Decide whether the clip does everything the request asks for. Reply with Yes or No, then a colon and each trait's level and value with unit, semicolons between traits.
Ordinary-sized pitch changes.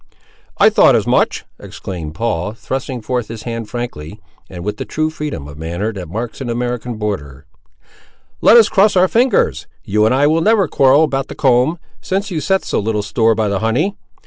No: wide, 6.3 semitones